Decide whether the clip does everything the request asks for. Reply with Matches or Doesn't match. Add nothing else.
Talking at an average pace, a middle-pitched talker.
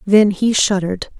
Doesn't match